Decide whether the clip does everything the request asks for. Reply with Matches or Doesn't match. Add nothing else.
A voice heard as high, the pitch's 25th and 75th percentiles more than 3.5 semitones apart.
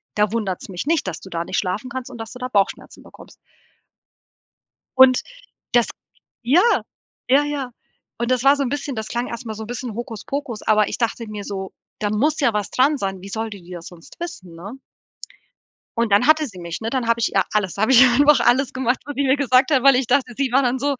Matches